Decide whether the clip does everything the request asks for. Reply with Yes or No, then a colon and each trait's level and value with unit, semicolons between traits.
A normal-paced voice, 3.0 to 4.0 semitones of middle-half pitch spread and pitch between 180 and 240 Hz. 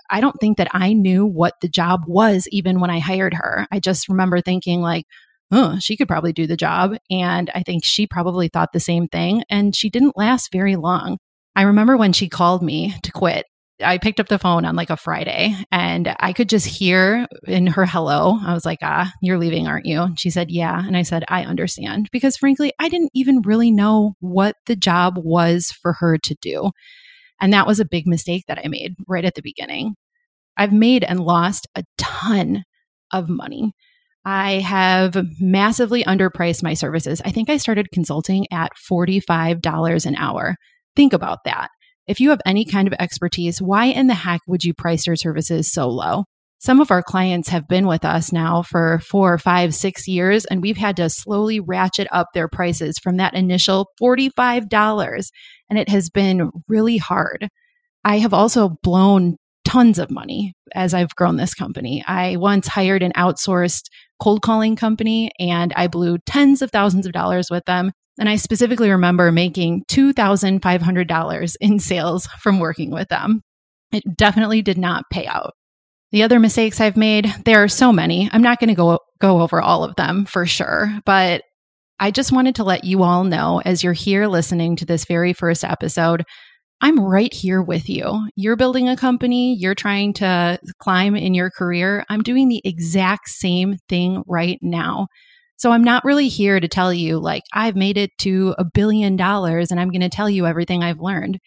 Yes: average, 190 wpm; average, 3.4 semitones; high, 190 Hz